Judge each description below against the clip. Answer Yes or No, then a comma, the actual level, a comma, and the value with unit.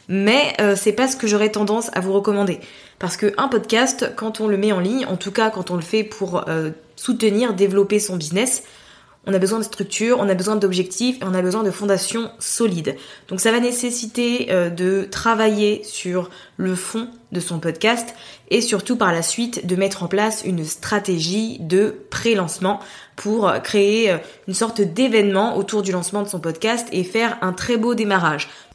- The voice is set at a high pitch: Yes, high, 205 Hz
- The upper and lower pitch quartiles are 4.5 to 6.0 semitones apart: No, average, 3.2 semitones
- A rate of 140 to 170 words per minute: No, average, 190 wpm